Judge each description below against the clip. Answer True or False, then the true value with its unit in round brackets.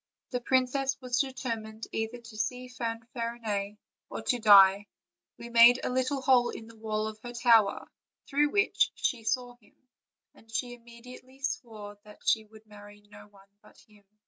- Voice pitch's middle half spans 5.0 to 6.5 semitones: False (2.7 semitones)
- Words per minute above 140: True (165 wpm)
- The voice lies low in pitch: False (230 Hz)